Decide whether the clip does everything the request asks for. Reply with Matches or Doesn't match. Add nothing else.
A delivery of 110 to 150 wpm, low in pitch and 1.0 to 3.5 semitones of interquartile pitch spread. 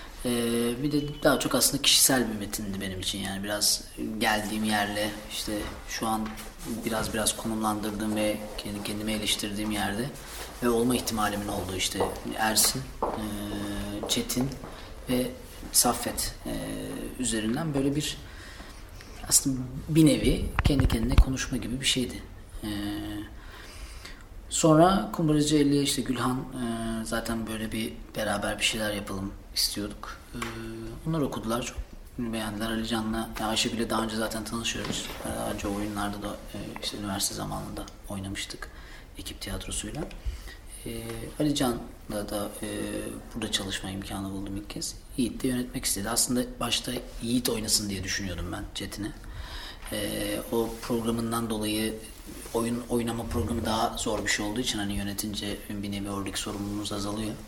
Matches